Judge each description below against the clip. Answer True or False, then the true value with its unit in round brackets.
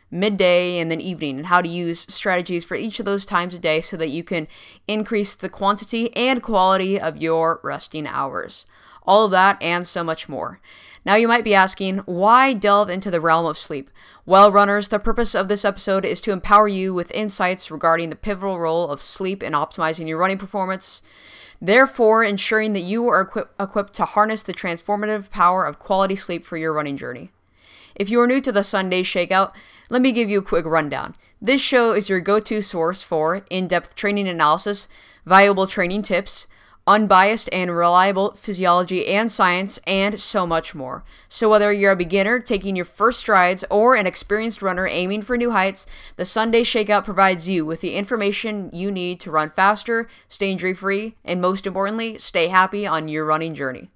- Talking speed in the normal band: True (190 wpm)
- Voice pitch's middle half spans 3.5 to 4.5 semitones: False (3.1 semitones)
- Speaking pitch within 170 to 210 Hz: True (190 Hz)